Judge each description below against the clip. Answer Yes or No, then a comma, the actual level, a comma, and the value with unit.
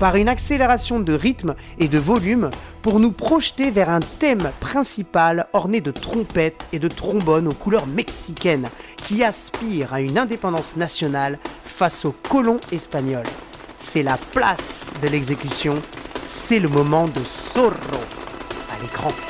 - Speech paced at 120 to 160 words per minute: Yes, slow, 145 wpm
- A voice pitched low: No, medium, 170 Hz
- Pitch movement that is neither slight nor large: No, wide, 7.1 semitones